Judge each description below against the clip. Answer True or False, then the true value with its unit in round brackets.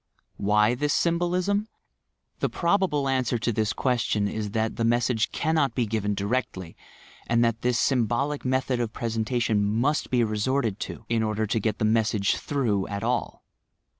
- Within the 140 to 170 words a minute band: True (160 wpm)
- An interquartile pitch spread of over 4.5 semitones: False (3.5 semitones)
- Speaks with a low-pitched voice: True (115 Hz)